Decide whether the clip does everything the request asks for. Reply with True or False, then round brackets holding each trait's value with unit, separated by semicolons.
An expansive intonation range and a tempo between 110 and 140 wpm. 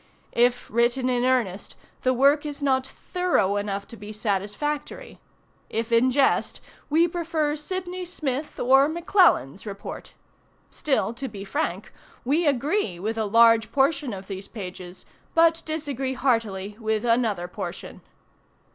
True (6.1 semitones; 135 wpm)